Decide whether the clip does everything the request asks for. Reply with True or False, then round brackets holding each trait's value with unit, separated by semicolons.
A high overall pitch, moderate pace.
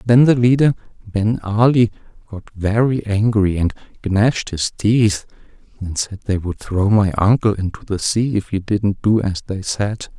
False (105 Hz; 170 wpm)